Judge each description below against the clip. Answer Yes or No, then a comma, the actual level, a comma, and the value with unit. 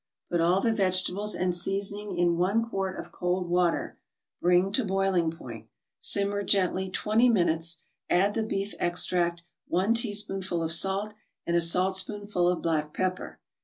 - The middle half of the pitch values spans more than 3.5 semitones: No, narrow, 2.5 semitones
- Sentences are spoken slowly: No, average, 150 wpm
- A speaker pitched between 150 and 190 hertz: Yes, medium, 185 Hz